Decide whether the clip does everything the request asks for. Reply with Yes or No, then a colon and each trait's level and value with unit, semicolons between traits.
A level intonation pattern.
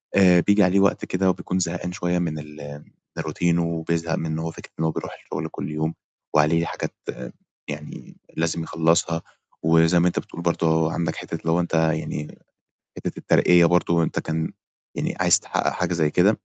Yes: narrow, 1.6 semitones